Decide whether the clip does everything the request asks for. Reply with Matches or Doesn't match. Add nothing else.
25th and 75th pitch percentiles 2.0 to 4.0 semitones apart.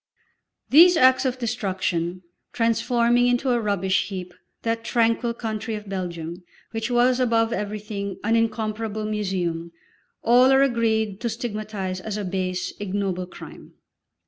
Matches